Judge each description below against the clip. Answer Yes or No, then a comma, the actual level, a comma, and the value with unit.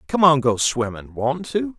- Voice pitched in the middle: Yes, medium, 145 Hz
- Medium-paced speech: Yes, average, 170 wpm